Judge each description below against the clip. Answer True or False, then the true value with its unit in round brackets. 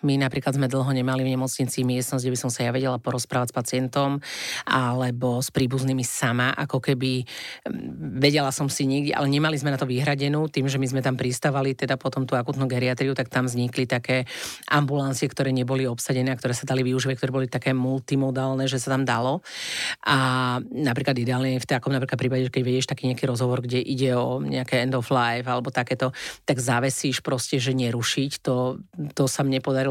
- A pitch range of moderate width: False (1.3 semitones)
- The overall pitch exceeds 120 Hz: True (130 Hz)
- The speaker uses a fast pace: True (195 wpm)